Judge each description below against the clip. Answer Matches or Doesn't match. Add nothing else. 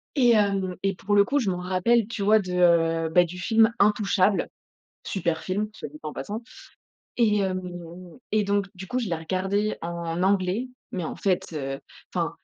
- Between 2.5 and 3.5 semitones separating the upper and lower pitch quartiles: Matches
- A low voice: Doesn't match